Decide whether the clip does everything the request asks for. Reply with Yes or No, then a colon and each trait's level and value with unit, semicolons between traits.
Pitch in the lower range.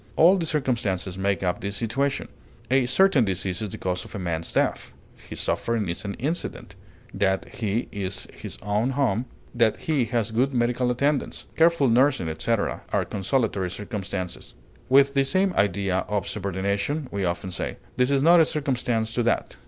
Yes: low, 115 Hz